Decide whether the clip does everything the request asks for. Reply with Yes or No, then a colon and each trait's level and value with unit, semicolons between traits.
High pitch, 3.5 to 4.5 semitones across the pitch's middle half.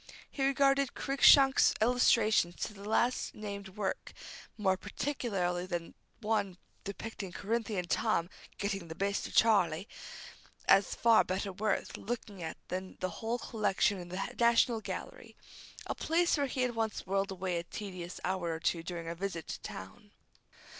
Yes: high, 200 Hz; average, 3.9 semitones